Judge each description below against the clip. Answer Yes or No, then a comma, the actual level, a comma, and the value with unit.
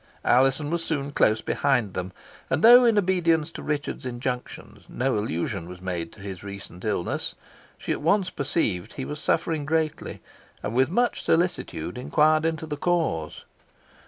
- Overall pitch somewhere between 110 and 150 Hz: Yes, medium, 140 Hz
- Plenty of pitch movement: Yes, wide, 8.0 semitones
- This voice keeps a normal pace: Yes, average, 160 wpm